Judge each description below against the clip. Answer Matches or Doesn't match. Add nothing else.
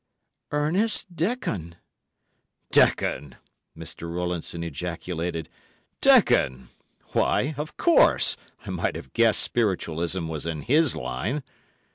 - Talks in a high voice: Doesn't match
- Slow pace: Matches